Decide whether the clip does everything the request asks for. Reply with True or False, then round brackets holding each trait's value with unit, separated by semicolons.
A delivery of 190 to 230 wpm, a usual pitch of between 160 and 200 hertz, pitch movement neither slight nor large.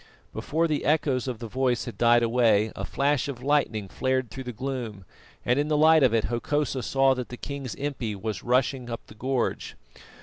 False (200 wpm; 130 Hz; 3.1 semitones)